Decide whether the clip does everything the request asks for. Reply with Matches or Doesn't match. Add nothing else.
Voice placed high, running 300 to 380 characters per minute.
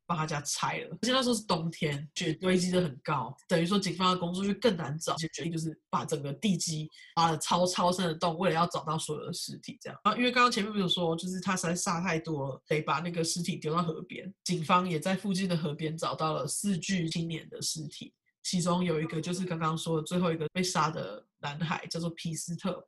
Doesn't match